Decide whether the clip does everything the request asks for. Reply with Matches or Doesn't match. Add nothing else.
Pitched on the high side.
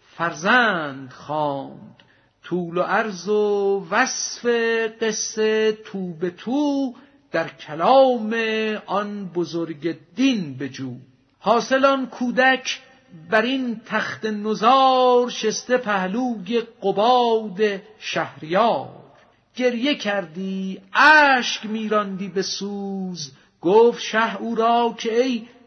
Matches